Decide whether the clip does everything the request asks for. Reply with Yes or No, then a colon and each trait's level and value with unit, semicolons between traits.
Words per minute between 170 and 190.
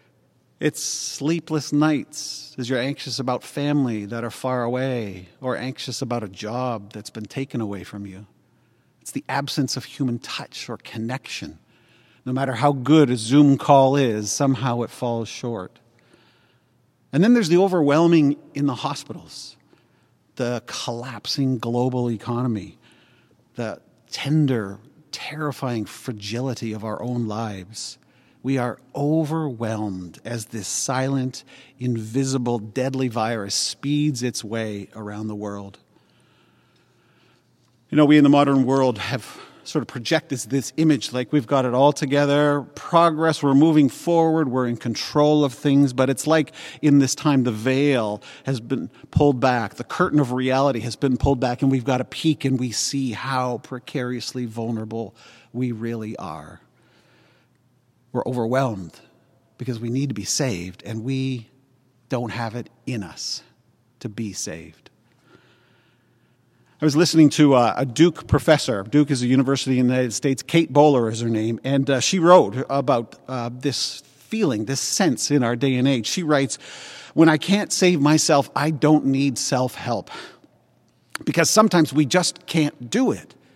No: average, 150 wpm